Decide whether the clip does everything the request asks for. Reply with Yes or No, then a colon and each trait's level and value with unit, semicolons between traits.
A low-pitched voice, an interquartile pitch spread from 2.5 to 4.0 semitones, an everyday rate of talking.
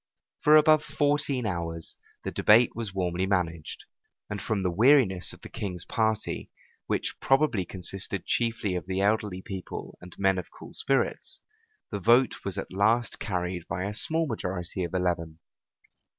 No: very low, 95 Hz; average, 4.4 semitones; average, 155 wpm